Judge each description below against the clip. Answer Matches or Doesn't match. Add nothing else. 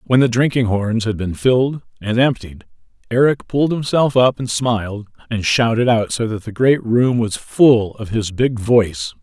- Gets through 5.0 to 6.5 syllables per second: Doesn't match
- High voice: Doesn't match